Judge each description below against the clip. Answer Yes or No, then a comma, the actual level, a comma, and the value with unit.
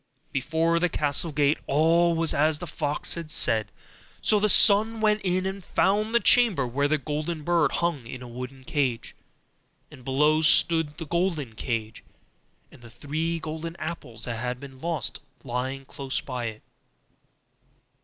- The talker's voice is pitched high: No, medium, 150 Hz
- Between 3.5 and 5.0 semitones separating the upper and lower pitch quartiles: Yes, average, 4.4 semitones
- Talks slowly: No, average, 165 wpm